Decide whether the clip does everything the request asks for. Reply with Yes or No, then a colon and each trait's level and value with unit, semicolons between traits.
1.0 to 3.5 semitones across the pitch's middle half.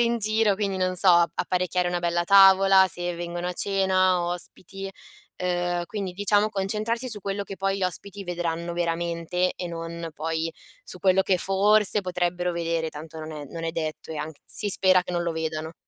Yes: narrow, 2.4 semitones